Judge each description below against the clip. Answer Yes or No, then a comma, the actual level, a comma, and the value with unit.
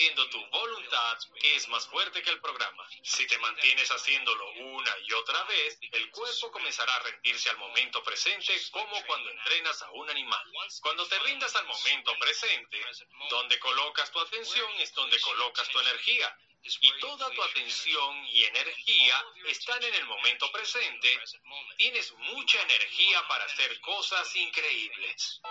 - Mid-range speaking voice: No, high, 235 Hz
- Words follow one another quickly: No, average, 150 wpm